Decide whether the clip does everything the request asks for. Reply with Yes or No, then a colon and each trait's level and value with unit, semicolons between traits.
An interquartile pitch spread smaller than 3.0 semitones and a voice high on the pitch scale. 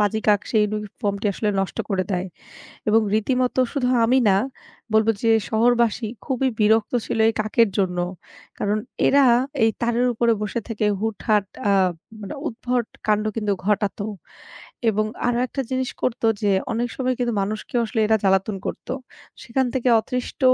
Yes: narrow, 2.6 semitones; high, 220 Hz